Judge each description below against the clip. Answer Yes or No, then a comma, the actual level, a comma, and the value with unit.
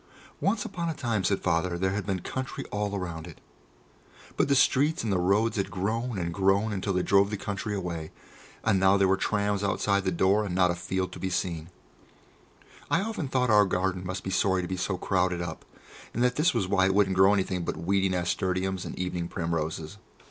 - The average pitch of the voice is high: No, very low, 95 Hz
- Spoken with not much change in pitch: Yes, narrow, 2.2 semitones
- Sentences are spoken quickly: Yes, fast, 215 wpm